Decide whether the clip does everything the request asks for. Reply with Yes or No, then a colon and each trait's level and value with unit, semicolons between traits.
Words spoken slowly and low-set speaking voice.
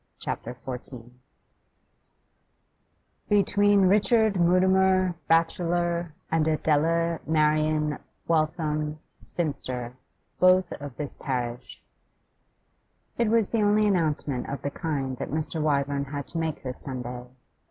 No: slow, 105 wpm; medium, 155 Hz